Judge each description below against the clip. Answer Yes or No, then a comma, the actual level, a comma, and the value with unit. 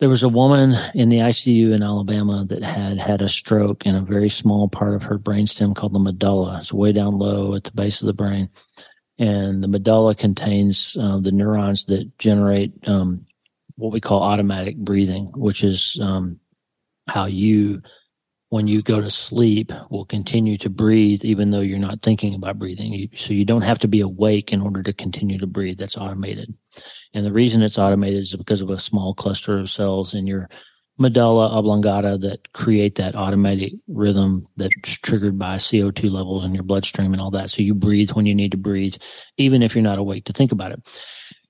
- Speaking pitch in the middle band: No, low, 100 Hz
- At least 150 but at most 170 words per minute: No, average, 200 wpm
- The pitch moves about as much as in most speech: No, narrow, 1.5 semitones